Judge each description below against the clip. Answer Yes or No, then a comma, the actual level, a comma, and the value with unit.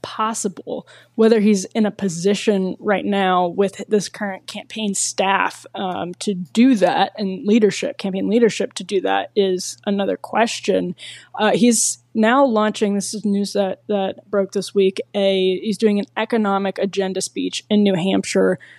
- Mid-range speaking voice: No, high, 200 Hz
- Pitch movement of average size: No, narrow, 1.9 semitones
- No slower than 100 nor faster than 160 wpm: Yes, average, 155 wpm